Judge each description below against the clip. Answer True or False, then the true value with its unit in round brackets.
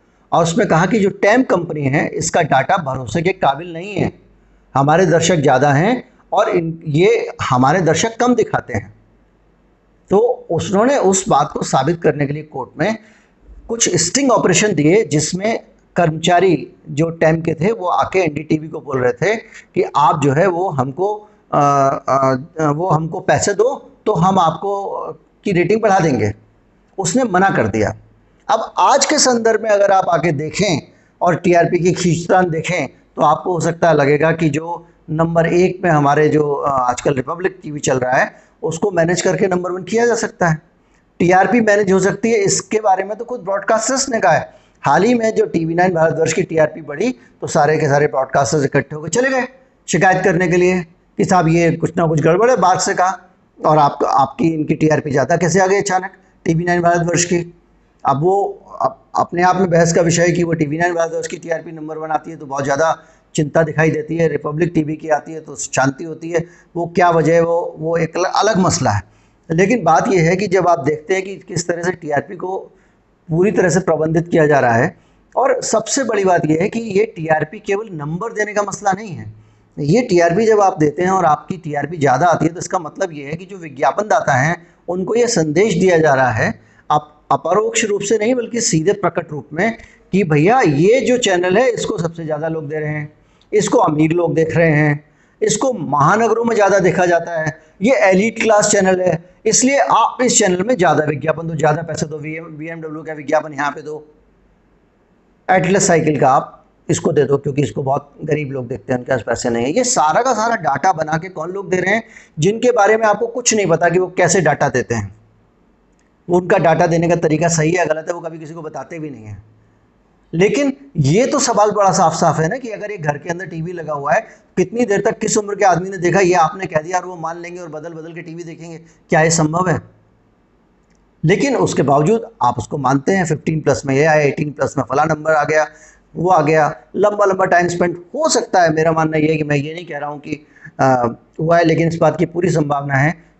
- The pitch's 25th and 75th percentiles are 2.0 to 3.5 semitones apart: False (4.0 semitones)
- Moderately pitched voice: True (170 Hz)